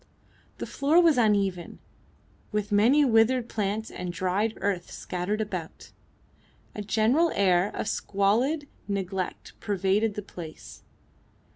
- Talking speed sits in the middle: No, slow, 115 wpm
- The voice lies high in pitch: Yes, high, 205 Hz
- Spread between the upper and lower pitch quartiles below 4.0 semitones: Yes, average, 2.9 semitones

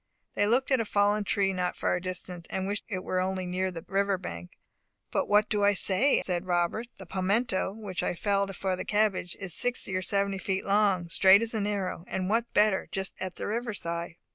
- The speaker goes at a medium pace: No, fast, 215 wpm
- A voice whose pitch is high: Yes, high, 195 Hz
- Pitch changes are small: Yes, narrow, 2.1 semitones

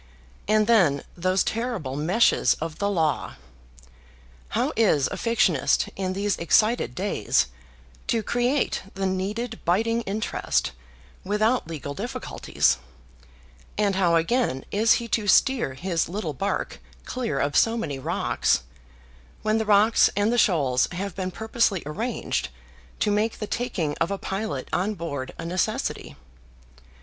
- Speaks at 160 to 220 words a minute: No, slow, 135 wpm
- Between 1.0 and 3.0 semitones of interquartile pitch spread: No, average, 5.2 semitones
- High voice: Yes, high, 200 Hz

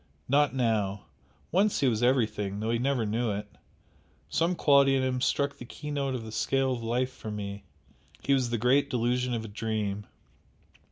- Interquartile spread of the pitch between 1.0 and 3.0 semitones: No, average, 3.7 semitones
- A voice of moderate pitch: No, low, 120 Hz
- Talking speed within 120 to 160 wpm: No, average, 180 wpm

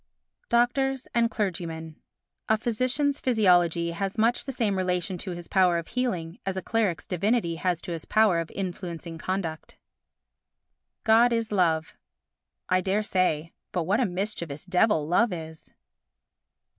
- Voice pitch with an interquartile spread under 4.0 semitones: No, average, 4.7 semitones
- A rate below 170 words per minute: Yes, average, 145 wpm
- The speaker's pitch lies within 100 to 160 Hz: No, medium, 185 Hz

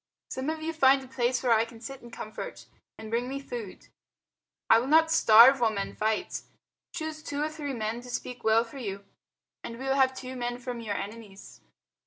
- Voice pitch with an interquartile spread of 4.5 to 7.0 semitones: No, average, 3.2 semitones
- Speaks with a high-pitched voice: Yes, high, 245 Hz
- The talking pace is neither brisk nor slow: No, fast, 210 wpm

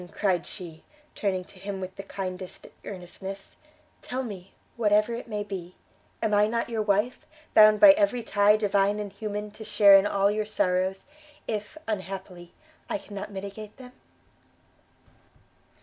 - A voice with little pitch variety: Yes, narrow, 1.9 semitones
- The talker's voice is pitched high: Yes, high, 205 Hz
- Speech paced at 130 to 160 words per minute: Yes, average, 150 wpm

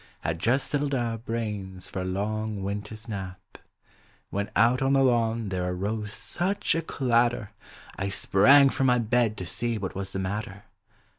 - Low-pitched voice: Yes, low, 110 Hz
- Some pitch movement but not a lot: Yes, average, 3.7 semitones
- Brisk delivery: No, average, 170 wpm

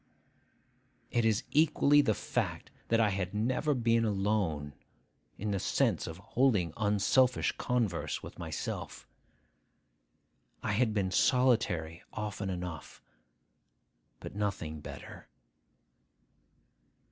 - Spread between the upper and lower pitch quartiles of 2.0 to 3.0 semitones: No, average, 4.2 semitones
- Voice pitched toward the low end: Yes, low, 105 Hz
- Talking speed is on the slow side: Yes, slow, 100 wpm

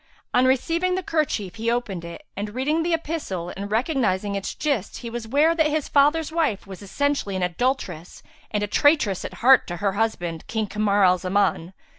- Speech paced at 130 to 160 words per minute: No, average, 190 wpm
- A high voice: Yes, high, 225 Hz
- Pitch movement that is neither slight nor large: No, wide, 6.9 semitones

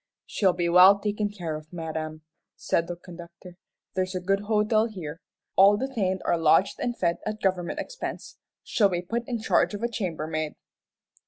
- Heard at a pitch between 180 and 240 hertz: Yes, medium, 185 Hz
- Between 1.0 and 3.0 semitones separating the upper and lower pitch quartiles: No, average, 3.6 semitones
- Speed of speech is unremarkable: Yes, average, 170 wpm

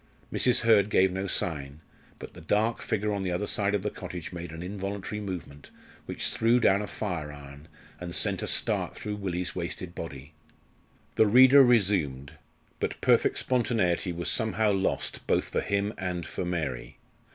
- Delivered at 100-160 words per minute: No, average, 170 wpm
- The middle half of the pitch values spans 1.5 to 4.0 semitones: Yes, average, 3.4 semitones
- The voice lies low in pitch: Yes, very low, 95 Hz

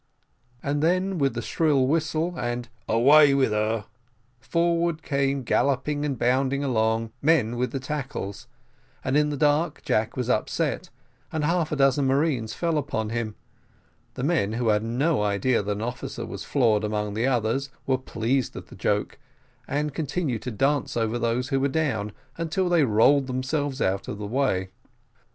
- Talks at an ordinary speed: Yes, average, 170 wpm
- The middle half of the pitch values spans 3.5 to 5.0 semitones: Yes, average, 4.7 semitones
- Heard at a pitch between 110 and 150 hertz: Yes, low, 135 Hz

